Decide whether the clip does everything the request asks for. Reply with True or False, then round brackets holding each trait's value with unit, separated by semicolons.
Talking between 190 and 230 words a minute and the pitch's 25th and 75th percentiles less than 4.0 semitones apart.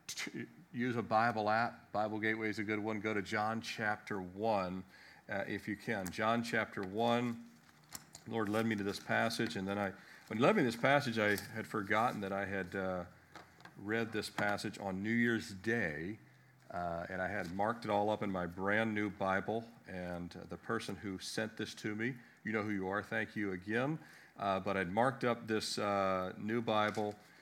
True (200 wpm; 2.6 semitones)